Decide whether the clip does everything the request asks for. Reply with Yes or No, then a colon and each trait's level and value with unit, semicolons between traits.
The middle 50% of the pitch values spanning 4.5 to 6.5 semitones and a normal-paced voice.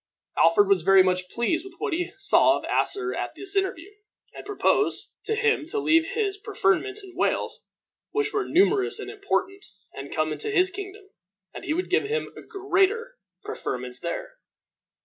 Yes: average, 5.1 semitones; average, 170 wpm